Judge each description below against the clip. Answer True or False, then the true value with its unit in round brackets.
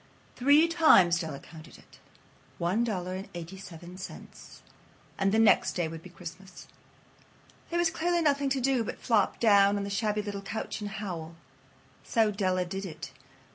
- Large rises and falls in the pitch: False (4.4 semitones)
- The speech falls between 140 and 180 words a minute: True (170 wpm)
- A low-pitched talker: False (200 Hz)